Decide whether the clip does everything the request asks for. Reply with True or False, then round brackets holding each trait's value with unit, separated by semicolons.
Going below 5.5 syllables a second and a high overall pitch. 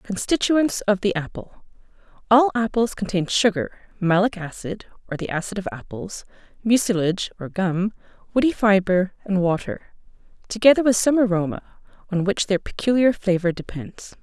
True (5.1 syllables/s; 200 Hz)